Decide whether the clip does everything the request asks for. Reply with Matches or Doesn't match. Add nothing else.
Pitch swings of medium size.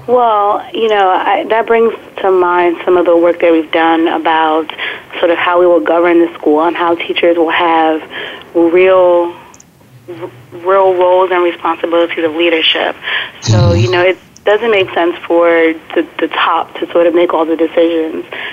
Doesn't match